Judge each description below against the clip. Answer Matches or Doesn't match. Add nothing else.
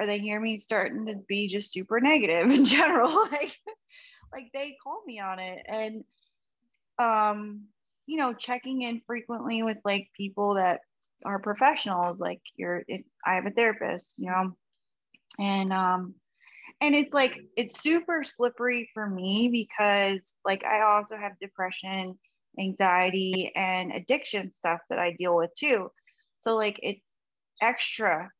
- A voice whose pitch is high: Matches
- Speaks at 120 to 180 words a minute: Matches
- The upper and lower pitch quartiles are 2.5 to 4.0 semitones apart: Doesn't match